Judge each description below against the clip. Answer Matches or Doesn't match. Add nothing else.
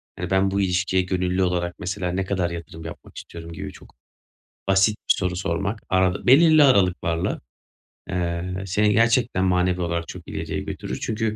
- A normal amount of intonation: Doesn't match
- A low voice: Matches